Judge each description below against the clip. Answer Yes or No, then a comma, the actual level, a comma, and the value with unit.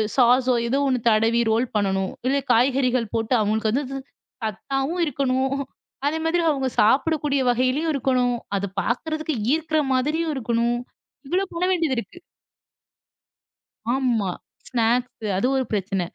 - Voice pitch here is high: Yes, very high, 255 Hz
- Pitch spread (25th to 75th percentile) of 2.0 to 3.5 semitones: No, average, 3.9 semitones